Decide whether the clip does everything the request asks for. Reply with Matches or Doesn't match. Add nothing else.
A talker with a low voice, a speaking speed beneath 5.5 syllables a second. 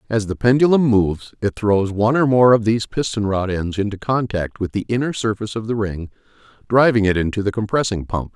Doesn't match